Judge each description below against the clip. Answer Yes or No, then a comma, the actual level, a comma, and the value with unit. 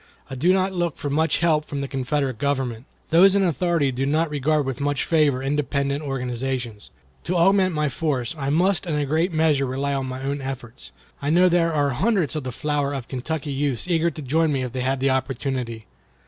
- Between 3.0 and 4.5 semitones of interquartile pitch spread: Yes, average, 3.4 semitones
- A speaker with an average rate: No, fast, 210 wpm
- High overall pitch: No, medium, 145 Hz